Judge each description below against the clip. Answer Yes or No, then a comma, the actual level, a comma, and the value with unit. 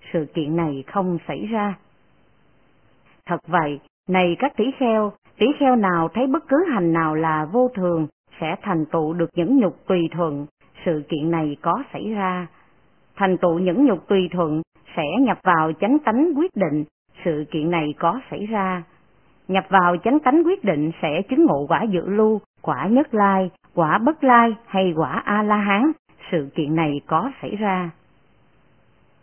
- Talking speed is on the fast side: No, average, 175 wpm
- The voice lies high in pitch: No, medium, 180 Hz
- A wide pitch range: No, average, 4.9 semitones